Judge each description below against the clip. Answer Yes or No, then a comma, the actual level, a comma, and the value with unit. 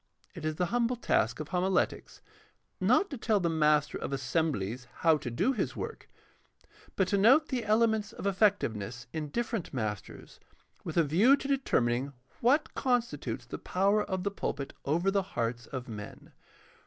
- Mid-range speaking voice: Yes, medium, 180 Hz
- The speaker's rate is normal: Yes, average, 170 wpm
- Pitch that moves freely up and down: Yes, wide, 8.2 semitones